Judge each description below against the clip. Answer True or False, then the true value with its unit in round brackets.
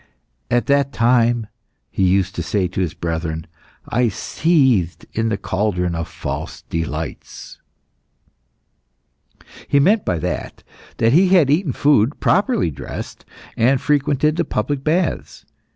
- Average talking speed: False (130 wpm)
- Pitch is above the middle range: False (120 Hz)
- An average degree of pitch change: False (7.8 semitones)